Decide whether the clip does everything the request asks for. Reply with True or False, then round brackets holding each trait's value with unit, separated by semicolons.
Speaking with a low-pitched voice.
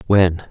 True (90 Hz)